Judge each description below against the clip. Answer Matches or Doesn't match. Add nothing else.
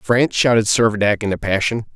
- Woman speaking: Doesn't match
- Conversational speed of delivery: Matches